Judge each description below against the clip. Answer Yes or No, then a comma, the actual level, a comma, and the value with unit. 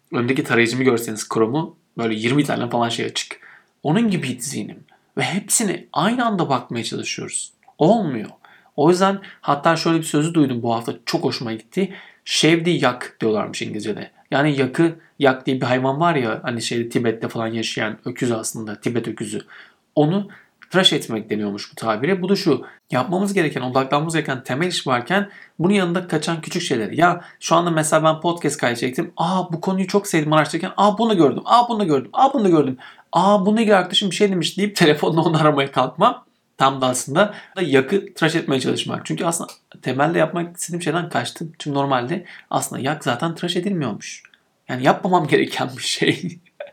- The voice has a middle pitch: Yes, medium, 160 Hz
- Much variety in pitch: Yes, wide, 6.0 semitones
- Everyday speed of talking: No, fast, 175 wpm